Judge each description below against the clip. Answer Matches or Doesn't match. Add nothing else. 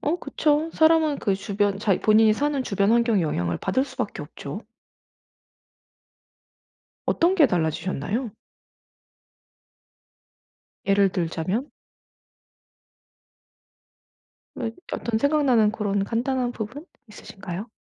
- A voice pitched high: Matches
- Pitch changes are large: Matches